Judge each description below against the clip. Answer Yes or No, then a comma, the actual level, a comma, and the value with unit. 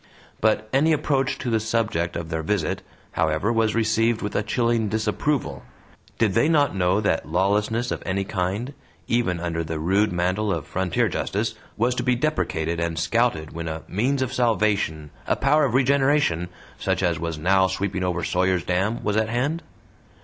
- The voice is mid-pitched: No, low, 105 Hz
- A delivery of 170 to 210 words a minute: Yes, average, 175 wpm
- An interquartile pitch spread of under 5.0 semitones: No, wide, 5.4 semitones